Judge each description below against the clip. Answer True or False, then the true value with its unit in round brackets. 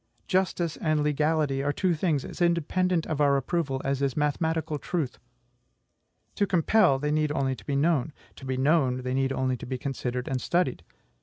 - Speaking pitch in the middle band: True (150 Hz)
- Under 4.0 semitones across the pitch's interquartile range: True (3.6 semitones)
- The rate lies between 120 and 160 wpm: False (180 wpm)